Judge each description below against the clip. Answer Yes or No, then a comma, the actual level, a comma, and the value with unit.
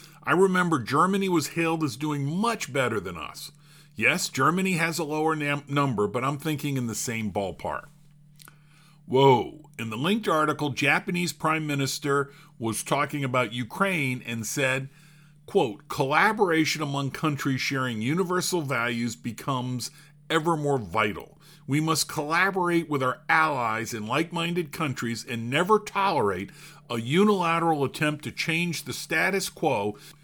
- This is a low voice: No, medium, 150 Hz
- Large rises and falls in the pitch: No, average, 3.6 semitones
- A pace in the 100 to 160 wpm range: Yes, average, 140 wpm